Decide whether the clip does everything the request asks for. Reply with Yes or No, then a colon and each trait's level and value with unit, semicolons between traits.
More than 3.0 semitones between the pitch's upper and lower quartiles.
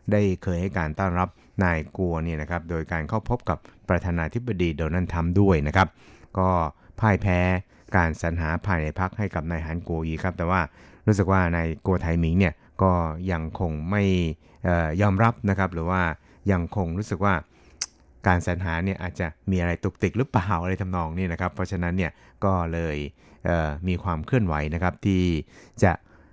No: narrow, 2.4 semitones